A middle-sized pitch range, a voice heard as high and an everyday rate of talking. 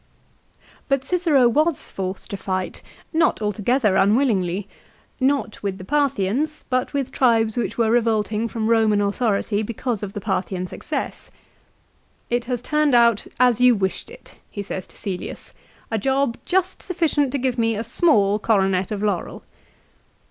Yes: average, 4.6 semitones; high, 230 Hz; average, 155 wpm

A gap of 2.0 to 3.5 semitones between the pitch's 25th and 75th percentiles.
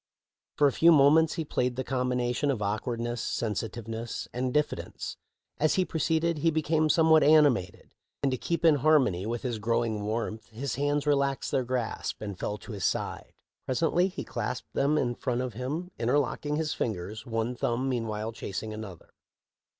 No: average, 4.7 semitones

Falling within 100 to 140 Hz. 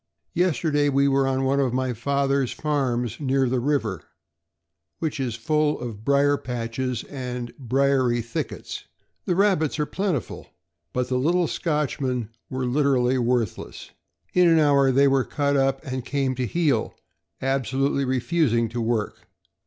Yes: low, 135 Hz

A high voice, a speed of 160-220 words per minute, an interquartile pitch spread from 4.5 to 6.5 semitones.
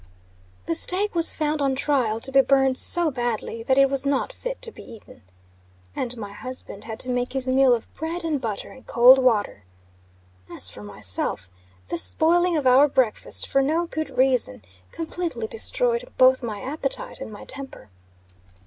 Yes: very high, 265 Hz; average, 175 wpm; average, 5.0 semitones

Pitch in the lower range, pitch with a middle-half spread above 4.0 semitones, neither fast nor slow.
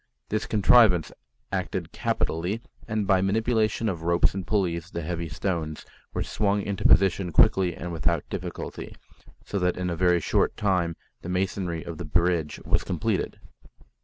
No: very low, 90 Hz; average, 2.8 semitones; average, 155 wpm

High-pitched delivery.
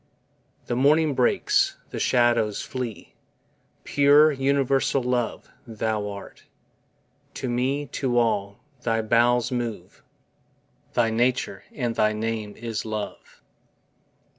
No: low, 120 Hz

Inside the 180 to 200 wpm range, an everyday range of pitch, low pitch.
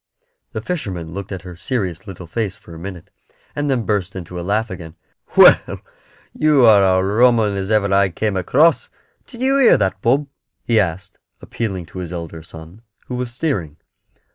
Yes: average, 185 wpm; average, 4.8 semitones; low, 100 Hz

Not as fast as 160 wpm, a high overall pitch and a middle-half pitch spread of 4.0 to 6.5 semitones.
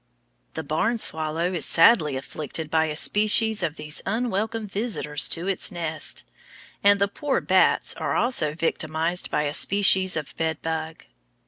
No: average, 150 wpm; medium, 165 Hz; average, 4.6 semitones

